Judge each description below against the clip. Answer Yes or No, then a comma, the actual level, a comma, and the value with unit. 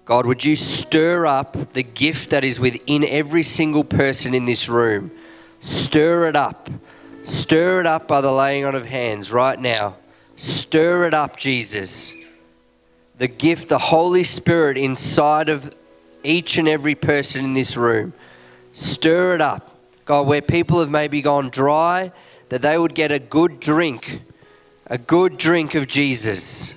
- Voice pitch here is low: No, medium, 145 Hz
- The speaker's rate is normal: Yes, average, 155 wpm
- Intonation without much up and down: No, average, 4.2 semitones